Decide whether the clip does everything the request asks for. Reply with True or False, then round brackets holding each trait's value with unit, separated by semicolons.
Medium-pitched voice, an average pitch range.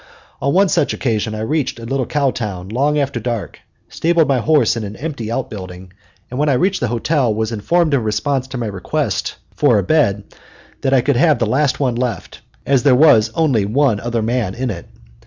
False (125 Hz; 4.5 semitones)